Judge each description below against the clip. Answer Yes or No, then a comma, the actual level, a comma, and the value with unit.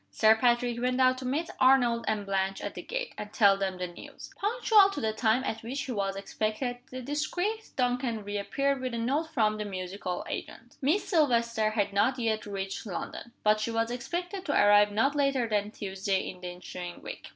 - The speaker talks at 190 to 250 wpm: Yes, average, 200 wpm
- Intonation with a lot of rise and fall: No, average, 4.4 semitones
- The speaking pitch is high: Yes, high, 230 Hz